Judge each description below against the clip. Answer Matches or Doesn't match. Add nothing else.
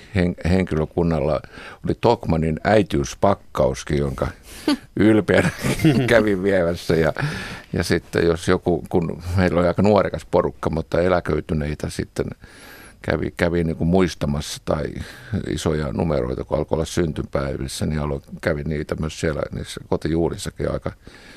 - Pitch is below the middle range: Matches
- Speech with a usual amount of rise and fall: Matches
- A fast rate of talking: Doesn't match